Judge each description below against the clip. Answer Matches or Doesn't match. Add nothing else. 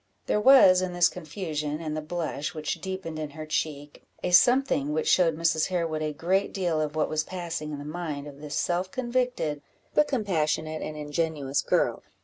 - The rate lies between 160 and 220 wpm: Matches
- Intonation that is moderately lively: Matches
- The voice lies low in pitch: Doesn't match